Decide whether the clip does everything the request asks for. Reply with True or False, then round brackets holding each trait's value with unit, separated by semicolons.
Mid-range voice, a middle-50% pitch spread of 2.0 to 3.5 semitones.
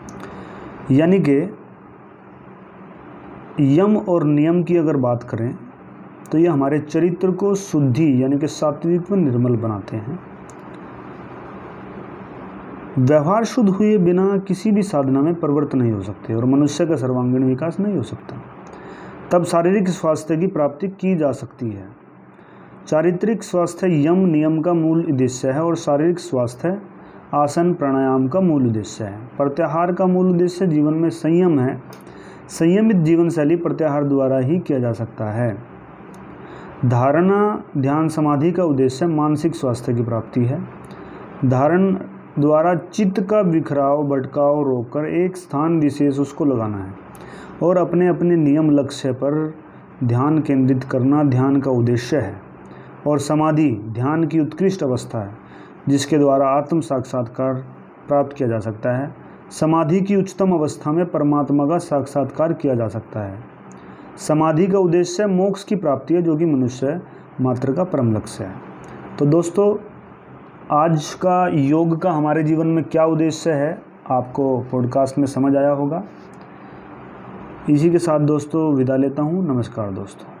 False (150 Hz; 4.6 semitones)